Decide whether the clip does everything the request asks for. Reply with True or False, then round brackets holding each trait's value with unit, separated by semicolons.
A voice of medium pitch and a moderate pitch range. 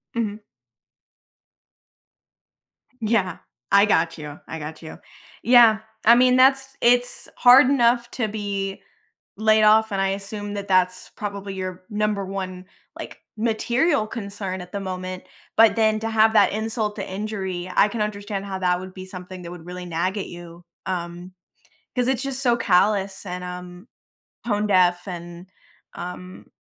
False (200 Hz; 3.3 semitones)